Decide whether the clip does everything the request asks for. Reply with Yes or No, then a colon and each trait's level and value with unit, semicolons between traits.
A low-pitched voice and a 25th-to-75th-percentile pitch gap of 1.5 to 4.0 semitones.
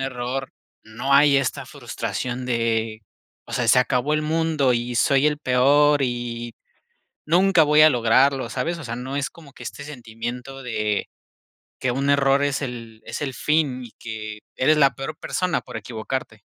Yes: low, 130 Hz; average, 3.3 semitones